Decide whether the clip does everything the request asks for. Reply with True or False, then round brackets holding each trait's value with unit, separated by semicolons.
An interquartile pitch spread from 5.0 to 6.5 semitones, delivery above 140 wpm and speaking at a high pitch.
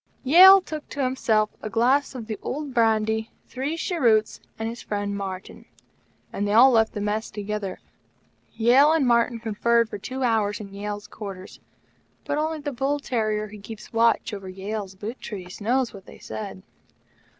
False (3.9 semitones; 170 wpm; 220 Hz)